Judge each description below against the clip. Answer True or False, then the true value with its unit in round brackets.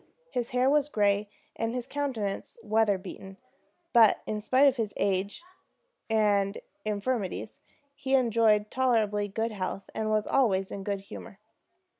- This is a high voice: True (215 Hz)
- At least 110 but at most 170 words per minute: True (140 wpm)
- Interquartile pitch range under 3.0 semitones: False (3.4 semitones)